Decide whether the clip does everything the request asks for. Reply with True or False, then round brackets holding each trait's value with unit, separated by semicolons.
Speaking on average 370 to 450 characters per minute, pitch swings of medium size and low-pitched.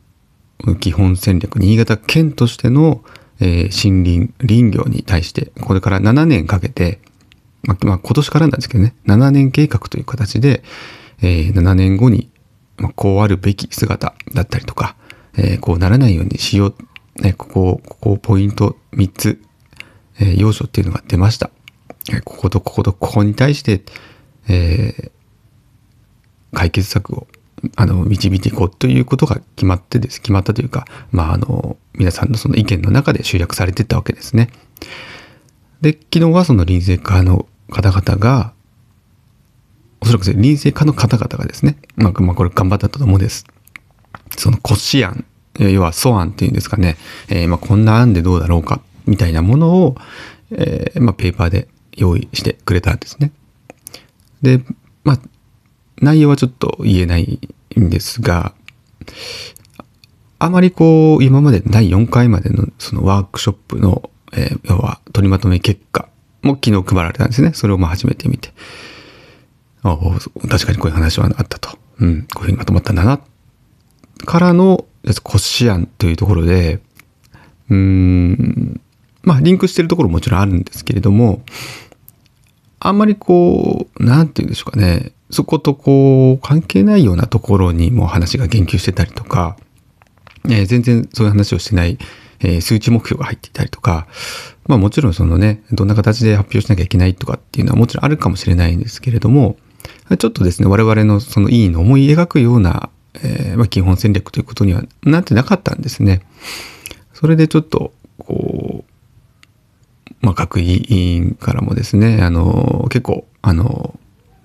False (325 characters per minute; 4.5 semitones; 110 Hz)